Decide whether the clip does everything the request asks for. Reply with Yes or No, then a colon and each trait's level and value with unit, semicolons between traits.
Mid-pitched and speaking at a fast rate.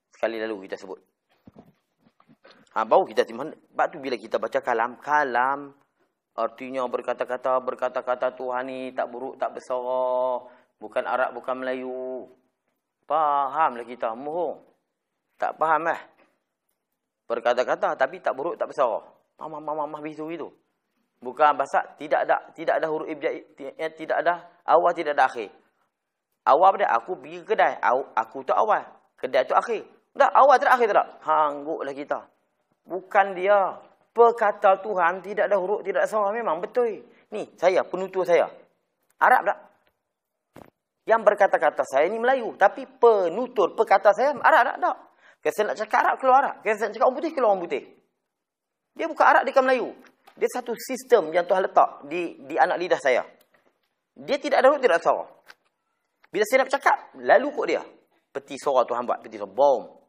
Yes: medium, 170 Hz; fast, 165 wpm